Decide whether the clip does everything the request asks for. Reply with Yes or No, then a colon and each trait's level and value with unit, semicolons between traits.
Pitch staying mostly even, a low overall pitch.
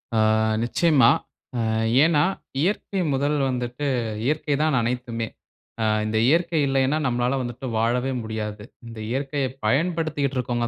No: average, 3.8 semitones; low, 130 Hz